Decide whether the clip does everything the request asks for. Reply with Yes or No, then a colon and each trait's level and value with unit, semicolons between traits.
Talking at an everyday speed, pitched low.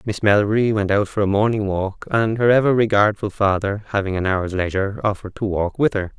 No: fast, 215 wpm; low, 105 Hz